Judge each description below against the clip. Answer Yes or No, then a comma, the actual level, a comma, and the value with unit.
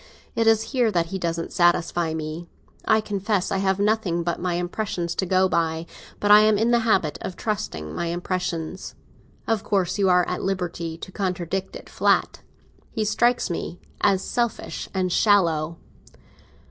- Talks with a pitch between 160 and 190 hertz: Yes, medium, 185 Hz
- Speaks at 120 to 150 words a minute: No, average, 165 wpm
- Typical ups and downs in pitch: Yes, average, 3.4 semitones